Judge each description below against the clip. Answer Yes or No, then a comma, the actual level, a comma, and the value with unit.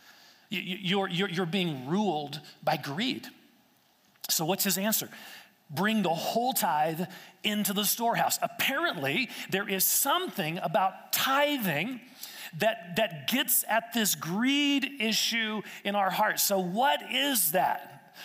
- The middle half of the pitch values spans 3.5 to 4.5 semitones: Yes, average, 3.8 semitones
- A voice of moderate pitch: No, high, 205 Hz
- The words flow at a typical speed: No, slow, 125 wpm